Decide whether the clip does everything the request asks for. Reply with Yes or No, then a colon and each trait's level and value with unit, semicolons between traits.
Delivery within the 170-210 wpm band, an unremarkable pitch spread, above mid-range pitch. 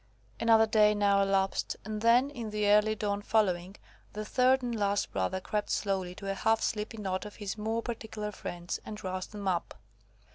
No: average, 185 wpm; narrow, 2.0 semitones; high, 210 Hz